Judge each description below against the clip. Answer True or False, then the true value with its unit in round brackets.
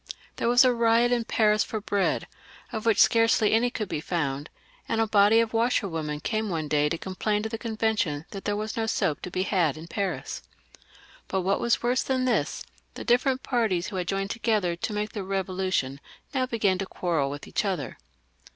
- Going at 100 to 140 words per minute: False (200 wpm)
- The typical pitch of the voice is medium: False (205 Hz)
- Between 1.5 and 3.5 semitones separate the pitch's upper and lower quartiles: False (4.2 semitones)